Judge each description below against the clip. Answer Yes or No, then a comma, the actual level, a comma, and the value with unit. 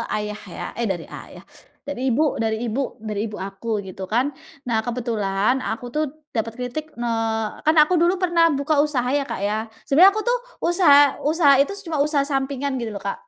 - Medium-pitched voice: No, very high, 250 Hz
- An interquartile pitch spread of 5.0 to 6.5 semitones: Yes, wide, 5.4 semitones